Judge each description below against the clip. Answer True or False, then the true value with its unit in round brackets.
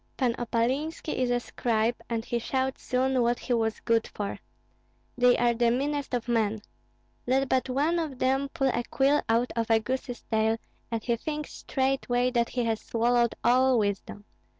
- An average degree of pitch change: False (2.3 semitones)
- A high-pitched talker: True (245 Hz)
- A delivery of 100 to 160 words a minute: False (175 wpm)